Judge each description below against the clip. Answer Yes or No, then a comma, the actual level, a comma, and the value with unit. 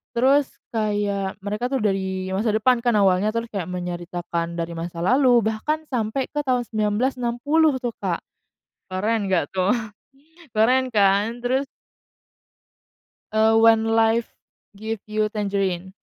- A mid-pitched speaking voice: No, high, 215 Hz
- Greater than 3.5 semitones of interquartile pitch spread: Yes, average, 3.9 semitones